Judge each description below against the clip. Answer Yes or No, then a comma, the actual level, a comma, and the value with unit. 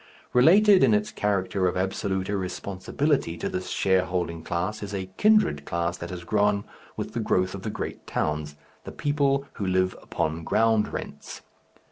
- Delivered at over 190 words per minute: No, average, 160 wpm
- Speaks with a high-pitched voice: No, very low, 95 Hz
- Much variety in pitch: No, average, 3.1 semitones